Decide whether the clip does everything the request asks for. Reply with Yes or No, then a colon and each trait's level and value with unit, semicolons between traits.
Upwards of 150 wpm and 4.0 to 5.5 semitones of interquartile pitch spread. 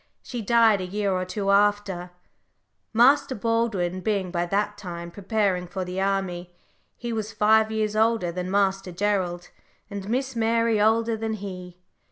No: average, 160 wpm; average, 3.3 semitones